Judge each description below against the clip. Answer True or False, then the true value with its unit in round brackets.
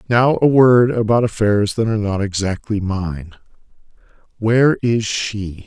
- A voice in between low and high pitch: False (110 Hz)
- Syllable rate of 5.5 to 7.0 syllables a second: False (4.4 syllables/s)